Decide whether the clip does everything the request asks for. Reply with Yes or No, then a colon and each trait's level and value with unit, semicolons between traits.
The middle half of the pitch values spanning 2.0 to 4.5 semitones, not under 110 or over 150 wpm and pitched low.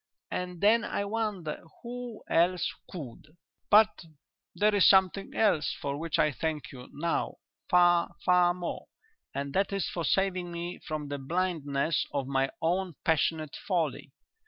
No: average, 4.0 semitones; average, 145 wpm; medium, 175 Hz